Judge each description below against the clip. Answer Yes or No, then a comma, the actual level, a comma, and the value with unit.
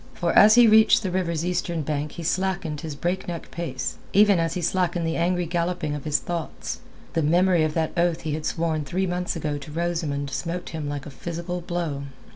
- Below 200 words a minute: No, fast, 205 wpm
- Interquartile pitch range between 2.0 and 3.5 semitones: Yes, narrow, 2.5 semitones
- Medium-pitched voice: Yes, medium, 170 Hz